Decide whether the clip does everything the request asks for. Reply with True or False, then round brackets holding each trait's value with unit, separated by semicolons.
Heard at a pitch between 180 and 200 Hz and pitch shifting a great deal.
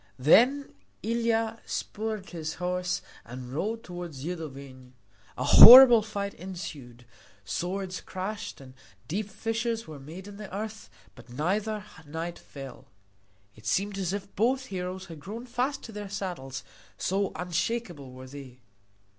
True (185 Hz; 6.4 semitones)